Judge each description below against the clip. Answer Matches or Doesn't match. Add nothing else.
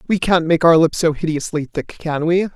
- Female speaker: Doesn't match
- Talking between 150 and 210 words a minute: Doesn't match